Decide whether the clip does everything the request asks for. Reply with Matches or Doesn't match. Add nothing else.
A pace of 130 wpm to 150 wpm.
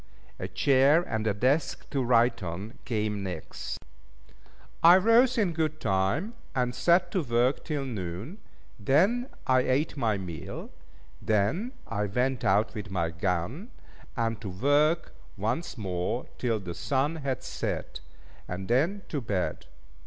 Matches